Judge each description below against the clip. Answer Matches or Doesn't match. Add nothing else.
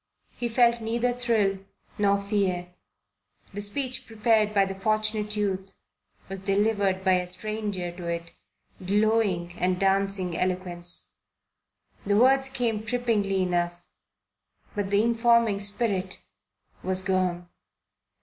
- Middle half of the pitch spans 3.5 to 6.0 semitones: Doesn't match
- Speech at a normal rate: Doesn't match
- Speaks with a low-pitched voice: Doesn't match